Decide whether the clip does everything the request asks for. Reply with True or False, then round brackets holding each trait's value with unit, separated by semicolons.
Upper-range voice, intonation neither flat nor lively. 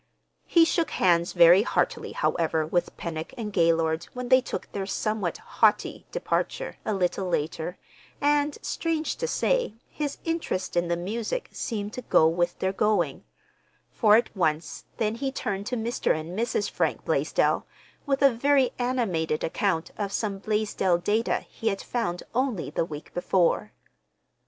False (205 Hz; 6.2 semitones)